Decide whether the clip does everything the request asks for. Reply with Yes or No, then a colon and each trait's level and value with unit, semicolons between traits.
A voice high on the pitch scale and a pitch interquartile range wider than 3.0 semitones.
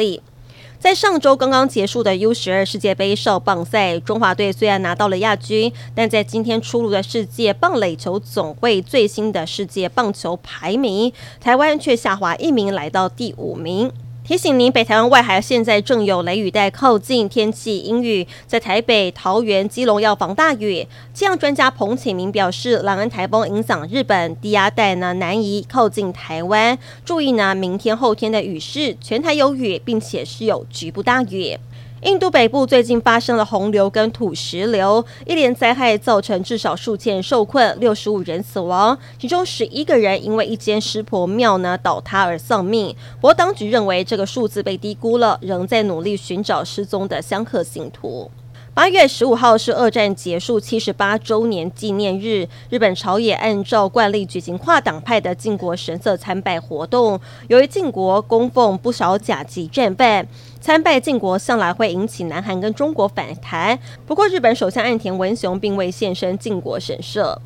Yes: high, 210 Hz; average, 3.8 semitones